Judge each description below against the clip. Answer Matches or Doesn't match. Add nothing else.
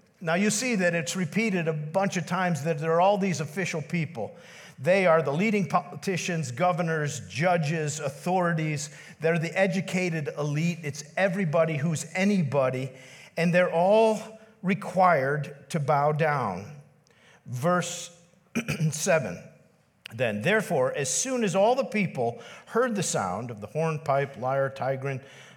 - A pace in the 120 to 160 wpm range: Matches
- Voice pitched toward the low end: Doesn't match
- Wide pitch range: Doesn't match